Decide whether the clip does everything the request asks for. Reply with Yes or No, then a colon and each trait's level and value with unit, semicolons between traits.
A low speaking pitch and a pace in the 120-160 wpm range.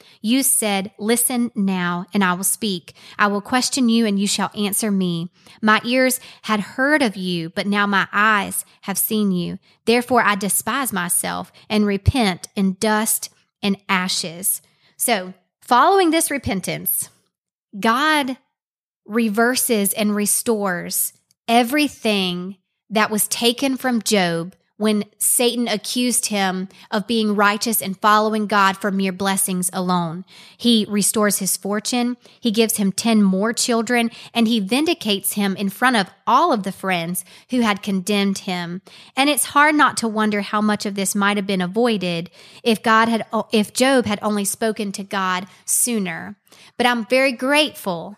No: high, 210 Hz; average, 150 wpm